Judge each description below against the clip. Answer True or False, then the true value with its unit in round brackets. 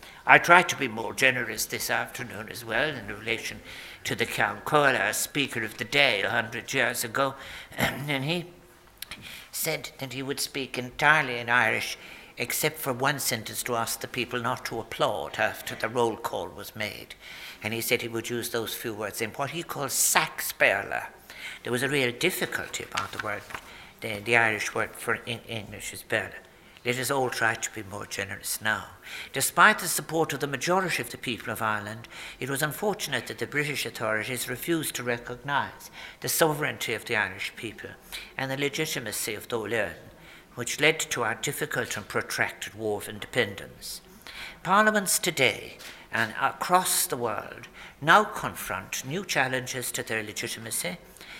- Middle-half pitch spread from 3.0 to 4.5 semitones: True (4.2 semitones)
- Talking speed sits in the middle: True (170 wpm)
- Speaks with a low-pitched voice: True (130 Hz)